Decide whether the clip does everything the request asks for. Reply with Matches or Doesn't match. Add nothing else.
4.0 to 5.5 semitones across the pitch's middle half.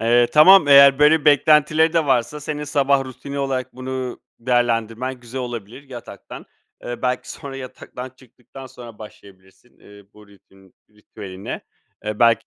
Doesn't match